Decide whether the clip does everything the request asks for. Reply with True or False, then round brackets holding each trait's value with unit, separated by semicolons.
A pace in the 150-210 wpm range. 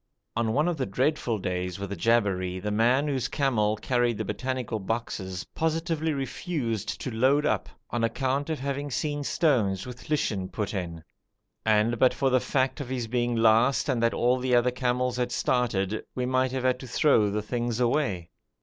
True (185 wpm)